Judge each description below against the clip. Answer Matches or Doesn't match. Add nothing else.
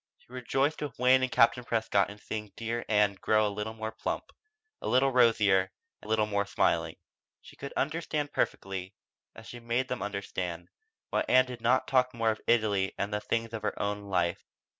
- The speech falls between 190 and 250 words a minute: Matches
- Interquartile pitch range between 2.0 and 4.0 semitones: Matches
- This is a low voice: Matches